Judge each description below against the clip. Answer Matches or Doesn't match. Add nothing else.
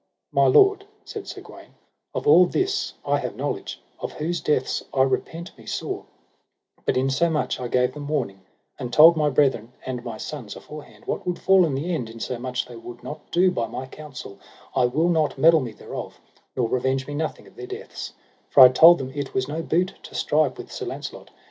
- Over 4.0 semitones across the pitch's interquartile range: Matches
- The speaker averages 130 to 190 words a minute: Doesn't match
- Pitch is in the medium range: Matches